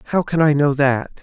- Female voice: No, male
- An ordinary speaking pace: No, fast, 245 wpm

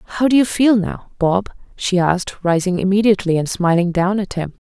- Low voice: No, high, 190 Hz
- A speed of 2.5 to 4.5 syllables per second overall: No, 5.7 syllables/s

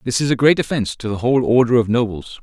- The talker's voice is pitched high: No, low, 120 Hz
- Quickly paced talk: Yes, fast, 270 wpm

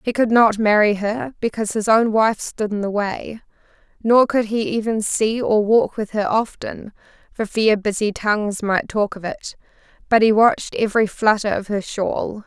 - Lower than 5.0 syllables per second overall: Yes, 4.7 syllables/s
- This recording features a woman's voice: Yes, female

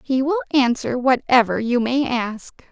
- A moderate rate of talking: Yes, average, 155 wpm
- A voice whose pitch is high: Yes, high, 245 Hz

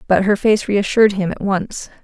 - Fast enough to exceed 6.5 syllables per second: No, 5.1 syllables/s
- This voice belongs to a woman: Yes, female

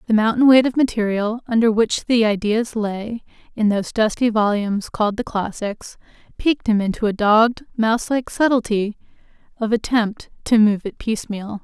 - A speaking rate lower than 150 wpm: No, average, 155 wpm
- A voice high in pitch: Yes, high, 220 Hz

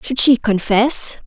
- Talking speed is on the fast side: No, average, 145 wpm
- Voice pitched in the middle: No, high, 230 Hz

